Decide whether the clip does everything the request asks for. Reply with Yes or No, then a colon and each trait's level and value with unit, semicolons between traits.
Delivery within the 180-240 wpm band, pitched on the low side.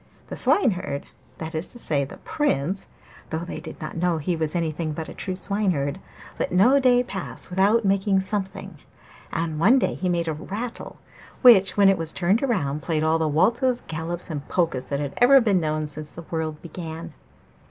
No: average, 190 wpm; medium, 175 Hz